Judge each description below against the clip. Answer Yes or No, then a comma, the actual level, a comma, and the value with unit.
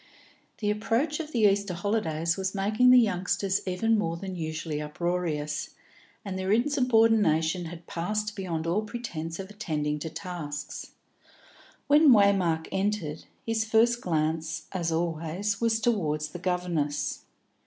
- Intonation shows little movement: No, average, 4.8 semitones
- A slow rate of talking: Yes, slow, 130 wpm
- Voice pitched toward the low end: No, medium, 185 Hz